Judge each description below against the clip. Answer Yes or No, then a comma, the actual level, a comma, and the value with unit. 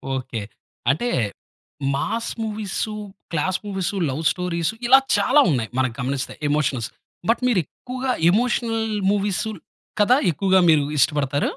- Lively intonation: Yes, wide, 8.0 semitones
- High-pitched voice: No, medium, 180 Hz